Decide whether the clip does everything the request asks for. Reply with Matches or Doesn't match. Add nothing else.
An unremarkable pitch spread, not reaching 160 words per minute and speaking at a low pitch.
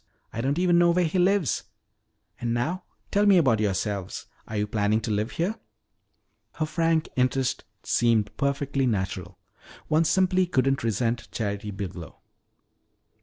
Doesn't match